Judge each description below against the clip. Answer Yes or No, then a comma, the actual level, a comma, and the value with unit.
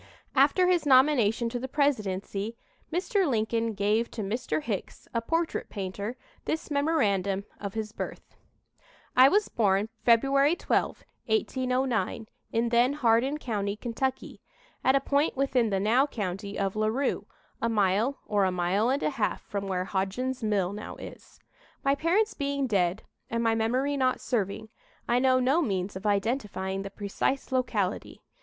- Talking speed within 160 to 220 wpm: No, average, 150 wpm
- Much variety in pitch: No, average, 5.0 semitones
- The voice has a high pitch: Yes, high, 230 Hz